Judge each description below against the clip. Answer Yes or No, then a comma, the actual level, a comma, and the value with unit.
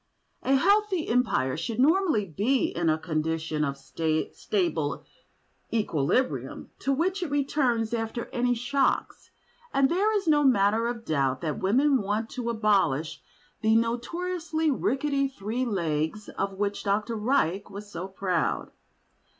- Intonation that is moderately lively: No, wide, 6.4 semitones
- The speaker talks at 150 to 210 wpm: No, slow, 135 wpm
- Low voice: No, high, 230 Hz